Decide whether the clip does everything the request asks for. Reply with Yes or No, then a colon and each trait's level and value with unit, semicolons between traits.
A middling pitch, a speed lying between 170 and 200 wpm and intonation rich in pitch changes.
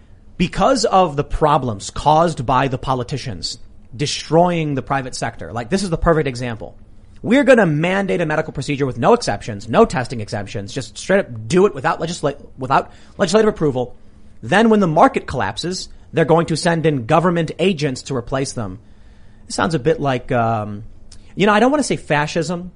Yes: medium, 145 Hz; average, 185 wpm; wide, 6.3 semitones